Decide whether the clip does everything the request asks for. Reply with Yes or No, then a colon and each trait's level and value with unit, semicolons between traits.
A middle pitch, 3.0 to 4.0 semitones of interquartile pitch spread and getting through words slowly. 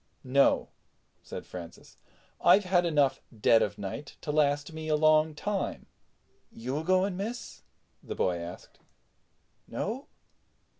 No: medium, 155 Hz; wide, 5.5 semitones; slow, 130 wpm